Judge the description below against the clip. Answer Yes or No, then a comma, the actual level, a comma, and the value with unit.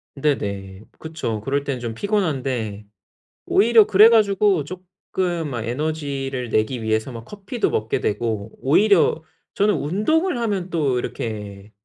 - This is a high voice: No, medium, 140 Hz